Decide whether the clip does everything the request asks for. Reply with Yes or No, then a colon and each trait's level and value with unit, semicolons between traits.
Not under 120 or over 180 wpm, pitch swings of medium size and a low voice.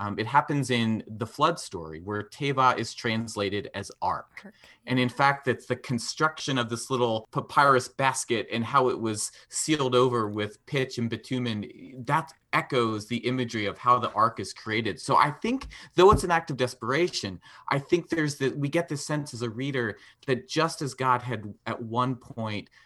No: average, 190 wpm; average, 3.6 semitones; low, 125 Hz